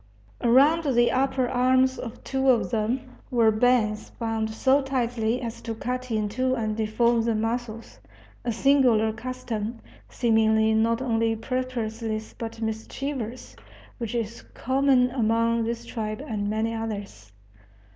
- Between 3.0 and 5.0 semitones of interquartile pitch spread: No, narrow, 2.4 semitones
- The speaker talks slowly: Yes, slow, 130 wpm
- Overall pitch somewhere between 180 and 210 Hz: No, high, 230 Hz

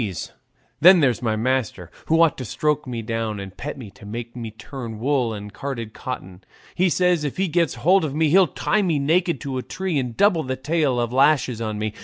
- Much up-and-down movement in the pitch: Yes, wide, 5.8 semitones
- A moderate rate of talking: No, fast, 220 wpm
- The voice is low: Yes, low, 130 Hz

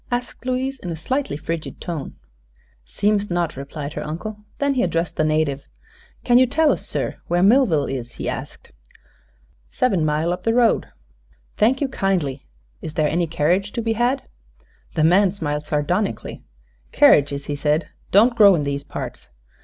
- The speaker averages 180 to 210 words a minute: No, average, 165 wpm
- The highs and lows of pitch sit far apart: Yes, wide, 7.1 semitones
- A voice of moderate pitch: Yes, medium, 175 Hz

